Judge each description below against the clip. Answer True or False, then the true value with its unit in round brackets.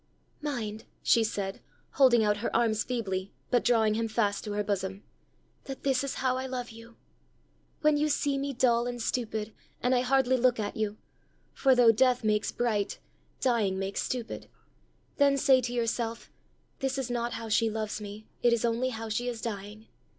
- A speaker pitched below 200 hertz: False (235 Hz)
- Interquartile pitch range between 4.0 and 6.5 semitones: False (2.9 semitones)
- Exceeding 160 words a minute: True (180 wpm)